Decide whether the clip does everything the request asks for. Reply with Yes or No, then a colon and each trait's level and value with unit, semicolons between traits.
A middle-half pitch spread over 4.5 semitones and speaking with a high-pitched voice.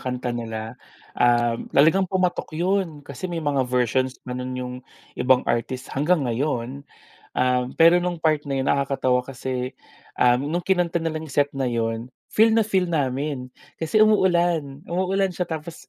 No: wide, 5.4 semitones; medium, 140 Hz